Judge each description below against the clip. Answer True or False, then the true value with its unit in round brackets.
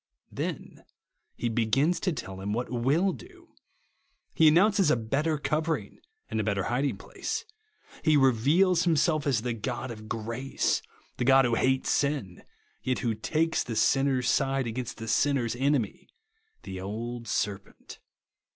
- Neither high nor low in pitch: False (130 Hz)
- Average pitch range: True (5.0 semitones)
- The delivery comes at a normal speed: True (150 wpm)